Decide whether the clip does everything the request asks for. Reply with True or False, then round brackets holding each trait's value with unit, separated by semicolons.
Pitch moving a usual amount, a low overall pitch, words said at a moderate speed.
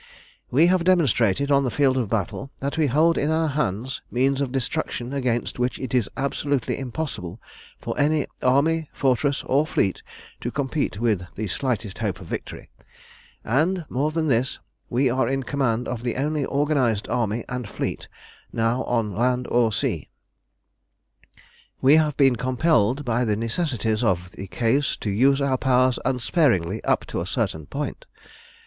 True (3.7 semitones; 130 Hz; 160 wpm)